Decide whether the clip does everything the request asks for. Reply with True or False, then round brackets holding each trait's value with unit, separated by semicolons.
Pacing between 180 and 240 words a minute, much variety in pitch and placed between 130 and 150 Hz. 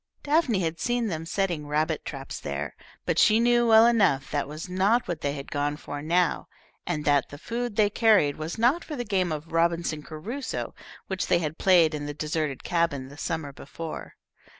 False (195 wpm; 6.0 semitones; 165 Hz)